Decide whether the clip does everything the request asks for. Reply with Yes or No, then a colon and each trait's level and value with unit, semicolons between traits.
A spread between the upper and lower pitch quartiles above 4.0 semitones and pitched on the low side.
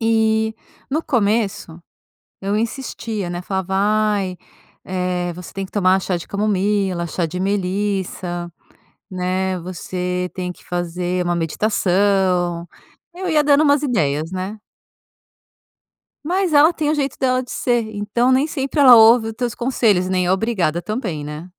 No: average, 4.4 semitones; high, 195 Hz